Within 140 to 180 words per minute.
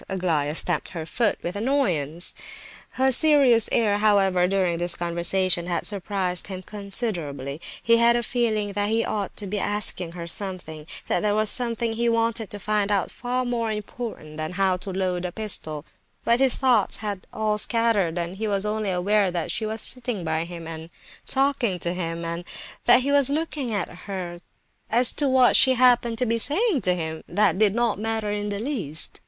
No: average, 190 wpm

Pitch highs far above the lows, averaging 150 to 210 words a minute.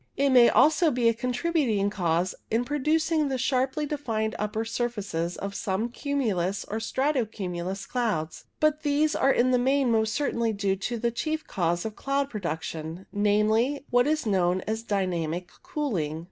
Yes: wide, 6.0 semitones; average, 170 wpm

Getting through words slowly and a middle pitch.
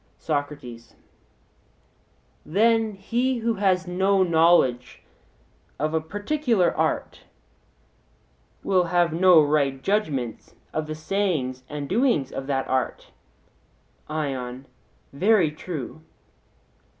Yes: slow, 95 wpm; medium, 160 Hz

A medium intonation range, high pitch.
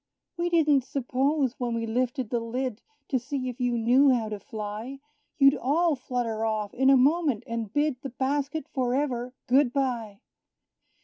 Yes: average, 3.1 semitones; very high, 255 Hz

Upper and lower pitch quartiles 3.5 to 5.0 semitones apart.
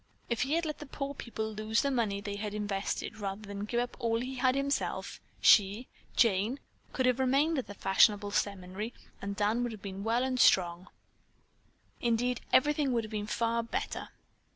Yes: average, 3.8 semitones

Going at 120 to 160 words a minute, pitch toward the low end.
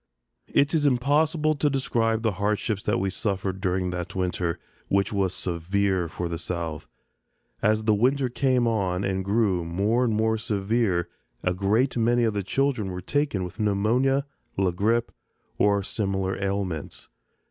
Yes: average, 155 wpm; low, 100 Hz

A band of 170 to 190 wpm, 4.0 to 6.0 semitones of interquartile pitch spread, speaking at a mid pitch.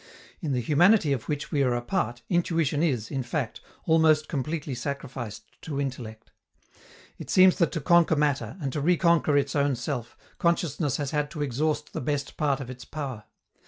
No: average, 180 wpm; average, 3.6 semitones; medium, 145 Hz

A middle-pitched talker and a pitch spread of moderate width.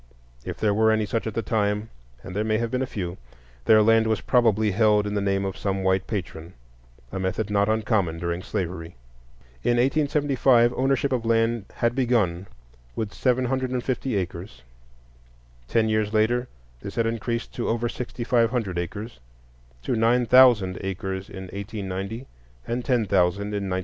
No: low, 110 Hz; average, 3.8 semitones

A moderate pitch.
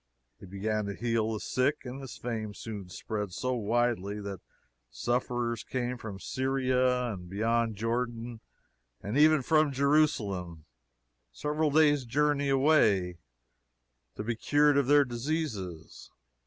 No: low, 120 Hz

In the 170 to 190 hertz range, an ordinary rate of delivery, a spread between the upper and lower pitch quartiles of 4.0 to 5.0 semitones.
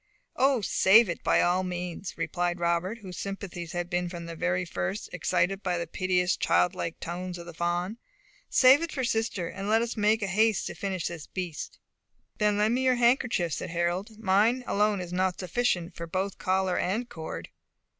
No: medium, 185 Hz; average, 180 wpm; average, 3.5 semitones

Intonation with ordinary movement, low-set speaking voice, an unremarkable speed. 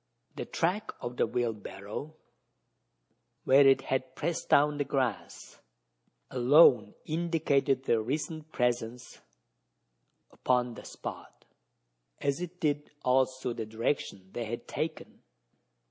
No: average, 3.6 semitones; low, 130 Hz; slow, 110 wpm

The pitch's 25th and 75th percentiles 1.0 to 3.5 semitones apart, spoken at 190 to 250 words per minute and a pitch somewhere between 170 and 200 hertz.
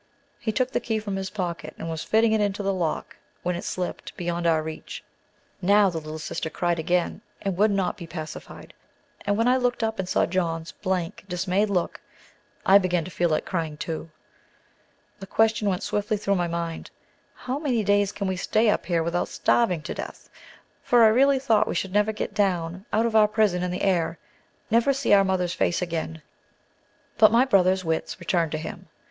No: average, 3.9 semitones; average, 200 wpm; high, 190 Hz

